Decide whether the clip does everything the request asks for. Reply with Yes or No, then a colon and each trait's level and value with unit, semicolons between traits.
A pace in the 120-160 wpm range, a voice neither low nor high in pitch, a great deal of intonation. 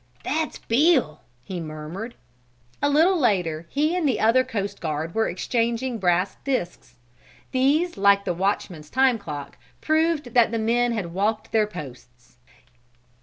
No: average, 140 wpm; high, 220 Hz; wide, 7.0 semitones